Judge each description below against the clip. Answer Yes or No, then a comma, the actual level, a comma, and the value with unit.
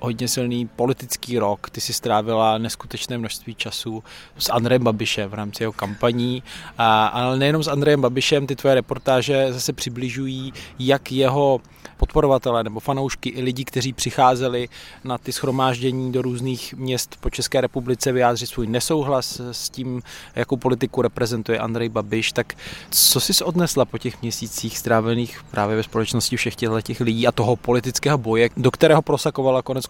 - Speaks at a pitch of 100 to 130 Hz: Yes, low, 125 Hz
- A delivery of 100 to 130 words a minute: No, average, 155 wpm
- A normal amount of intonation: No, narrow, 2.2 semitones